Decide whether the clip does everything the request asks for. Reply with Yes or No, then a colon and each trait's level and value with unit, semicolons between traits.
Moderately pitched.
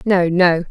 Yes: medium, 180 Hz